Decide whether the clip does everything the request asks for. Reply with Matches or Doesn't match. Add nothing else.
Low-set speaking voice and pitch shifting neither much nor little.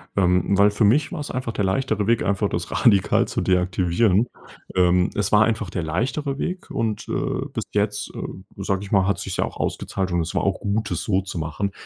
Matches